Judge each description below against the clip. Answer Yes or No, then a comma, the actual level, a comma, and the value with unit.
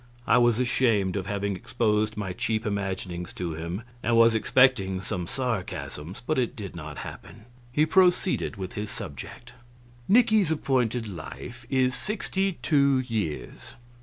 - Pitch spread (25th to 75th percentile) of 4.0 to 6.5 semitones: Yes, average, 5.2 semitones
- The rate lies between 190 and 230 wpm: No, average, 140 wpm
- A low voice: Yes, low, 110 Hz